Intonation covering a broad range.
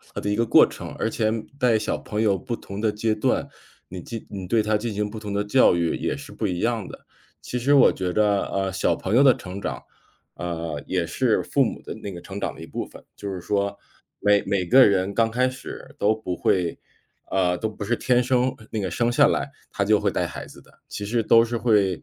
No: average, 3.3 semitones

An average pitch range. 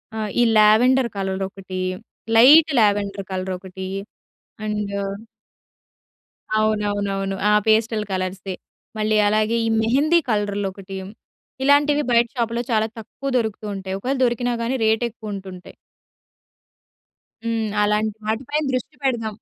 Yes: average, 3.1 semitones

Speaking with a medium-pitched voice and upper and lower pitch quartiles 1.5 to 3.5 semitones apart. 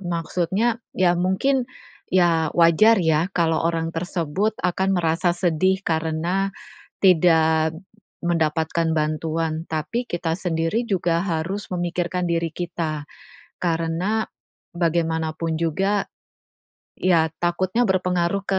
Yes: medium, 170 Hz; narrow, 2.5 semitones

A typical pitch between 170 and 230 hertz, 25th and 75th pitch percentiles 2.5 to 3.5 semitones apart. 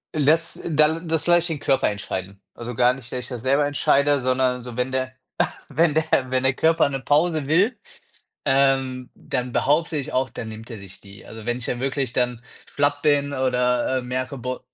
No: low, 130 Hz; average, 2.8 semitones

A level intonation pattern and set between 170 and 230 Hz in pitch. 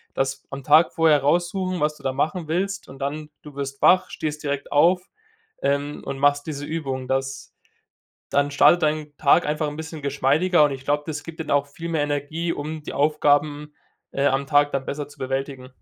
No: narrow, 2.1 semitones; medium, 145 Hz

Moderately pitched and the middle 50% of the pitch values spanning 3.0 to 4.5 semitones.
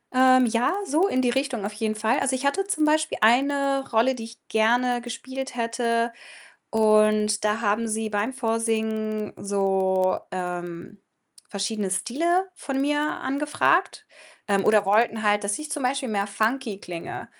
No: high, 230 Hz; average, 4.1 semitones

